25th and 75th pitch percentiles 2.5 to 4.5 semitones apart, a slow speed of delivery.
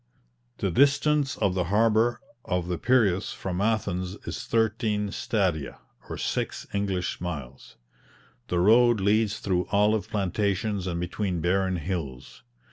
Yes: average, 3.5 semitones; slow, 125 wpm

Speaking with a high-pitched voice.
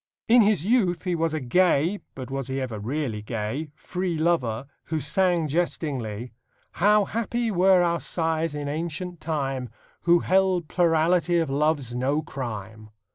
No: medium, 160 Hz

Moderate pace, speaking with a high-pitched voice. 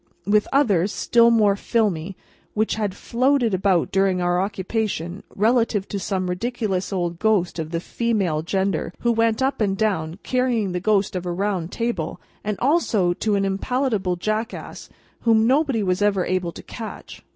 Yes: average, 160 wpm; high, 200 Hz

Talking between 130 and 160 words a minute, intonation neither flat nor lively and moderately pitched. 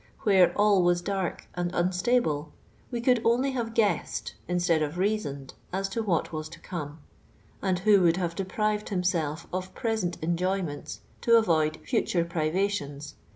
Yes: average, 155 wpm; average, 4.0 semitones; medium, 180 Hz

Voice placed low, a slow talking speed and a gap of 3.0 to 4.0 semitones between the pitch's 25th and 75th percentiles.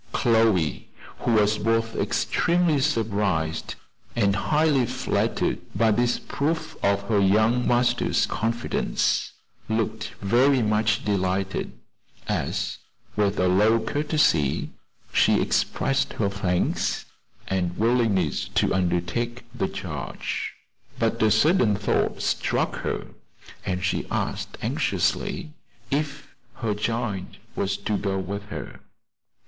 Yes: low, 110 Hz; slow, 110 wpm; average, 3.5 semitones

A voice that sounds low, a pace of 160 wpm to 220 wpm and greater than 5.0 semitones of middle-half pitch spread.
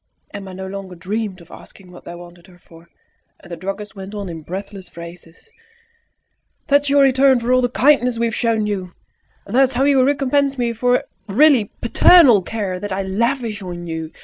No: high, 205 Hz; average, 200 wpm; wide, 5.6 semitones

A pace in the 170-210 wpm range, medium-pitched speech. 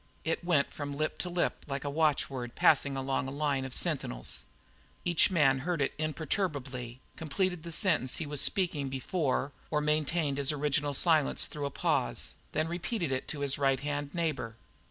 Yes: average, 175 wpm; medium, 145 Hz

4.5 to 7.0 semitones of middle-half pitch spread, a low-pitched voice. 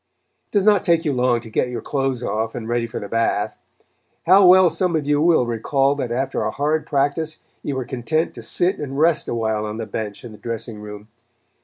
Yes: wide, 5.5 semitones; low, 130 Hz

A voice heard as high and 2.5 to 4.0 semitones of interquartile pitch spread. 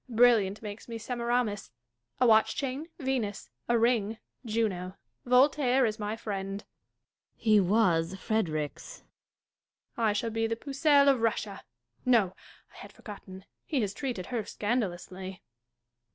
Yes: high, 220 Hz; average, 3.7 semitones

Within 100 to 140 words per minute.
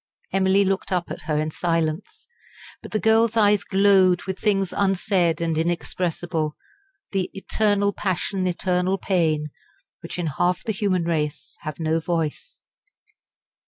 Yes: slow, 135 wpm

